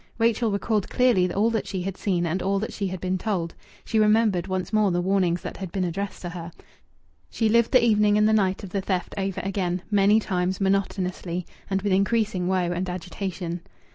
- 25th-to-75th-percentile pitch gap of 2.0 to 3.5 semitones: Yes, narrow, 2.6 semitones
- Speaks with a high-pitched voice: Yes, high, 195 Hz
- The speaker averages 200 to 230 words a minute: Yes, fast, 205 wpm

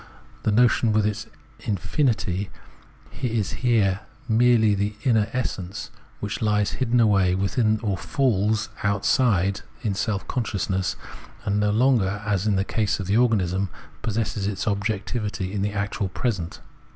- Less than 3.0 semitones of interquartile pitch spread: Yes, narrow, 2.5 semitones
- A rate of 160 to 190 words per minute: No, average, 140 wpm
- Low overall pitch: Yes, low, 105 Hz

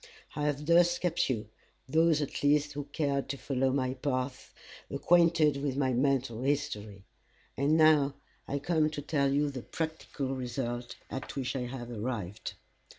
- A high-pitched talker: No, medium, 140 Hz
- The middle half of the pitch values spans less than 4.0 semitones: Yes, narrow, 2.5 semitones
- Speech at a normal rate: Yes, average, 155 wpm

